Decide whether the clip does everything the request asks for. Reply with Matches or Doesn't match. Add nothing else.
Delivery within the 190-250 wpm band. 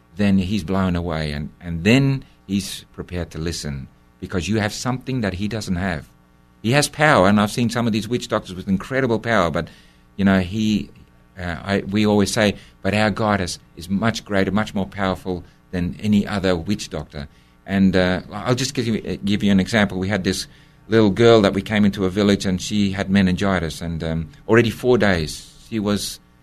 Matches